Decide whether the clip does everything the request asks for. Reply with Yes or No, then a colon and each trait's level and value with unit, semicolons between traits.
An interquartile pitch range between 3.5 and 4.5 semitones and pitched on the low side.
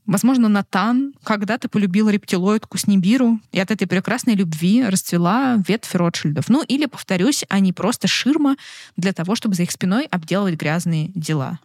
No: average, 4.0 semitones; high, 200 Hz